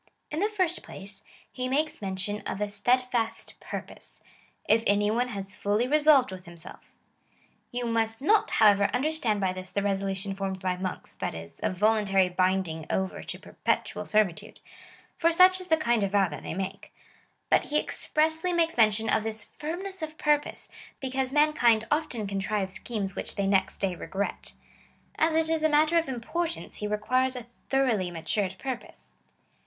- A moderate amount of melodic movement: No, wide, 7.4 semitones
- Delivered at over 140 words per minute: Yes, average, 180 wpm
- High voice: Yes, high, 220 Hz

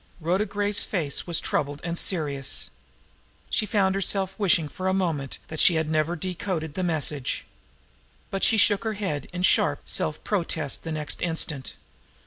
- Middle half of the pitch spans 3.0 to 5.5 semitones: Yes, average, 3.9 semitones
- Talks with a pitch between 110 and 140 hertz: No, medium, 170 Hz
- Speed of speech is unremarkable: Yes, average, 160 wpm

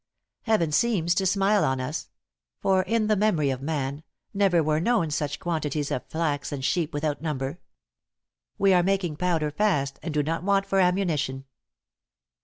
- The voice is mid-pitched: Yes, medium, 165 Hz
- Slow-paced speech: No, average, 165 wpm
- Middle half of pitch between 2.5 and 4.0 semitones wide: No, average, 4.8 semitones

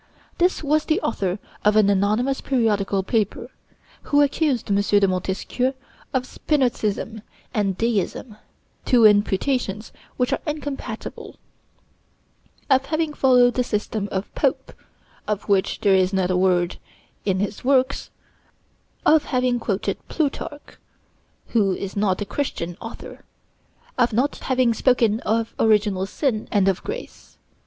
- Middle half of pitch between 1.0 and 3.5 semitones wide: No, average, 4.7 semitones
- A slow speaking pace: Yes, slow, 130 wpm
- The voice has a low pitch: No, high, 220 Hz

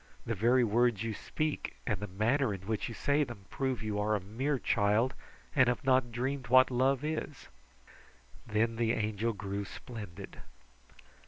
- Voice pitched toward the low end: Yes, low, 115 Hz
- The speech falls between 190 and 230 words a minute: No, average, 170 wpm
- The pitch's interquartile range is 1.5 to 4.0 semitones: Yes, average, 3.6 semitones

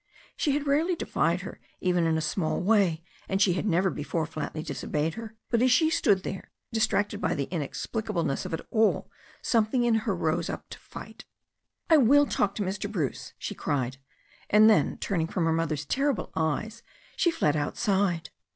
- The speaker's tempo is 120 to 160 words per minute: No, average, 180 wpm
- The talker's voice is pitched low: No, high, 195 Hz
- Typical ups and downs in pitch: No, wide, 5.8 semitones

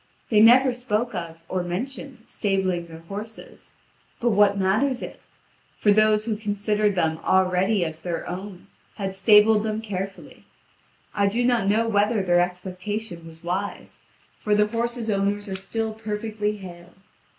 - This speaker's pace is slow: No, average, 150 wpm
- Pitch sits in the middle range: No, high, 205 Hz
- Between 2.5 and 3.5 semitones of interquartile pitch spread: Yes, average, 2.9 semitones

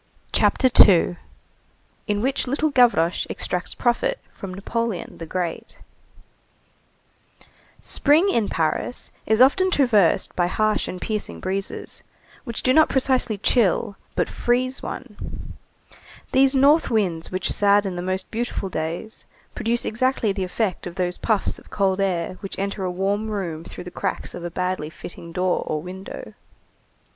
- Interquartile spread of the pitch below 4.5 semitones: No, average, 5.0 semitones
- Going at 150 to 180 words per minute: No, average, 140 wpm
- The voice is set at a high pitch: Yes, high, 200 Hz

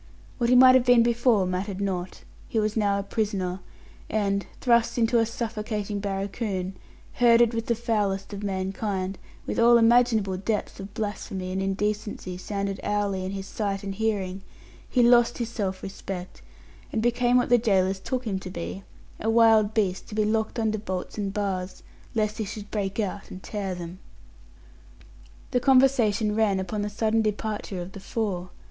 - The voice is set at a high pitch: Yes, high, 210 Hz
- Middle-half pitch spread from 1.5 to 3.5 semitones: Yes, average, 2.8 semitones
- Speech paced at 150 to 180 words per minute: Yes, average, 170 wpm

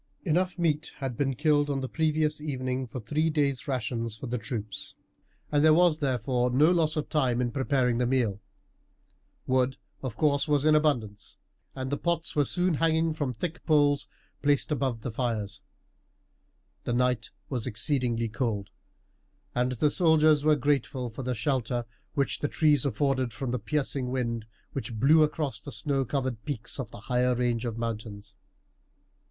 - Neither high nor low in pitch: No, low, 130 Hz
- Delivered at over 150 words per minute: Yes, average, 165 wpm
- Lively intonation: No, average, 3.7 semitones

